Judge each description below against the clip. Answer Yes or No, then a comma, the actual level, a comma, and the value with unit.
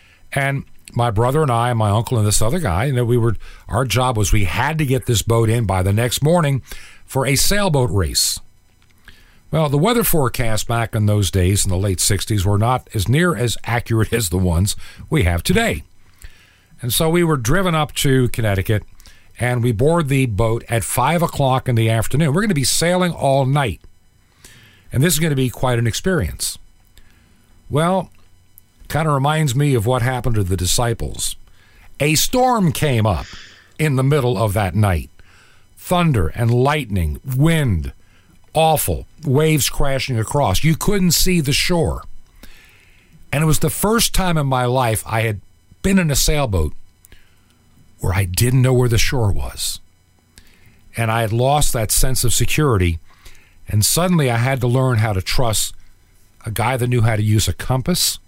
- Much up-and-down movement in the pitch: Yes, wide, 6.8 semitones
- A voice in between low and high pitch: No, low, 115 Hz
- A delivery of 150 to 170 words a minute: No, average, 180 wpm